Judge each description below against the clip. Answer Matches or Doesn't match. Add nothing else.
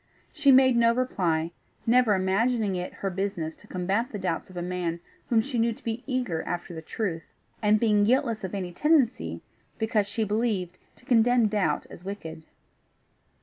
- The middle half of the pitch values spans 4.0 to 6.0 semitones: Matches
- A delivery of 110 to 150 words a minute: Doesn't match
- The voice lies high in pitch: Matches